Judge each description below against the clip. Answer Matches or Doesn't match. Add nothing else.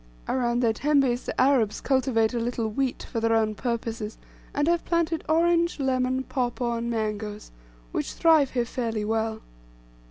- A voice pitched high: Matches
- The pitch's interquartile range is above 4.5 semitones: Doesn't match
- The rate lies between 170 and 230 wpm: Doesn't match